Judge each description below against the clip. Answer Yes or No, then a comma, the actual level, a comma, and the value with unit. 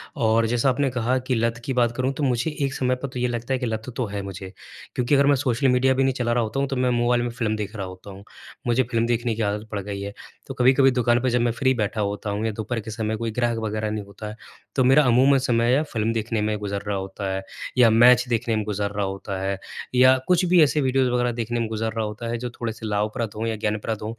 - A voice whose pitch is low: Yes, low, 115 Hz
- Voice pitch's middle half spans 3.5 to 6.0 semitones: No, average, 2.8 semitones